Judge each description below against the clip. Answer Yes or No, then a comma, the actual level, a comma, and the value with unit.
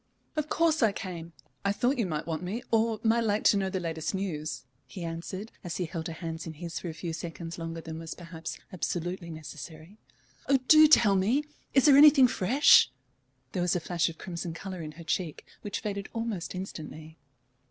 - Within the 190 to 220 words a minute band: Yes, average, 200 wpm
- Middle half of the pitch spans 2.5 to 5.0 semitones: Yes, average, 4.5 semitones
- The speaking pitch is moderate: Yes, medium, 180 Hz